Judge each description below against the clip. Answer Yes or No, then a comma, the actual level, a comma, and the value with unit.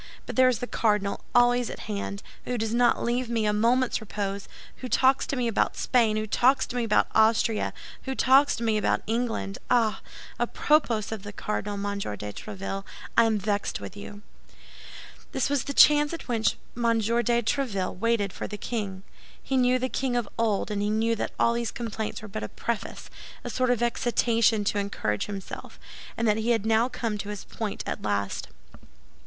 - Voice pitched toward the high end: Yes, high, 225 Hz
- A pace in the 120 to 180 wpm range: No, average, 195 wpm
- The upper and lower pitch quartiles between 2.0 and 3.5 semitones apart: Yes, average, 2.9 semitones